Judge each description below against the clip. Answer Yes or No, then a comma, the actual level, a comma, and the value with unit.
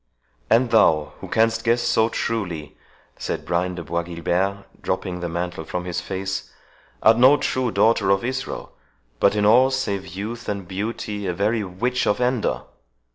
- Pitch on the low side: Yes, low, 100 Hz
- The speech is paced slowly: No, average, 165 wpm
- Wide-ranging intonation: No, average, 4.4 semitones